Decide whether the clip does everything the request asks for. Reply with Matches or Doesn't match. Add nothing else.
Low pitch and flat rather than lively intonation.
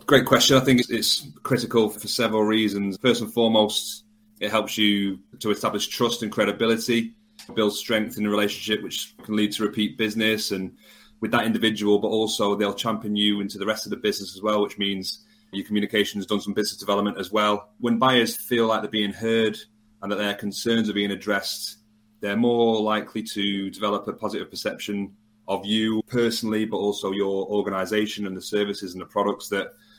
Matches